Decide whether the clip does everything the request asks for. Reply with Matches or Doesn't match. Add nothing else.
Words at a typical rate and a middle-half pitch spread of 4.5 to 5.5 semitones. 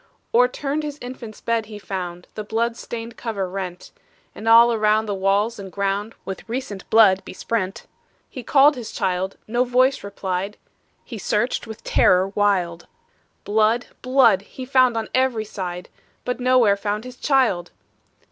Doesn't match